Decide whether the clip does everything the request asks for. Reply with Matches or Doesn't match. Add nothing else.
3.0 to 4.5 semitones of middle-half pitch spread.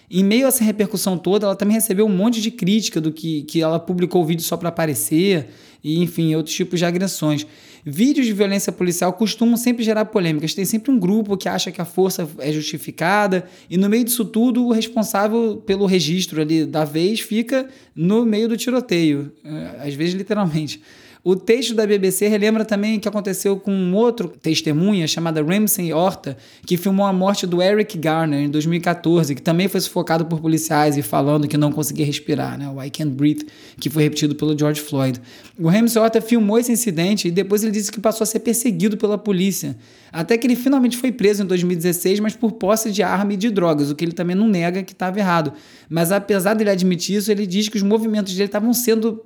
Doesn't match